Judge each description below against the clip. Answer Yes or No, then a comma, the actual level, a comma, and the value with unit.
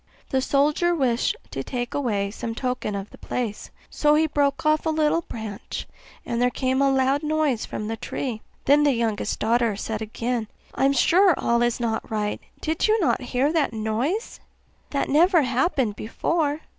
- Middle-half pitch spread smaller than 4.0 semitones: No, average, 4.8 semitones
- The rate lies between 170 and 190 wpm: Yes, average, 180 wpm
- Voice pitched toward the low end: No, very high, 255 Hz